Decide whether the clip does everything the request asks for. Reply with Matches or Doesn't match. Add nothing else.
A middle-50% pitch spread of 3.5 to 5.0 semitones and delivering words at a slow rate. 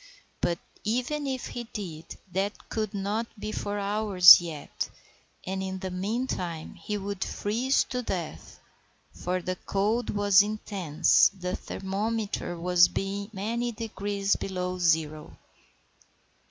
Doesn't match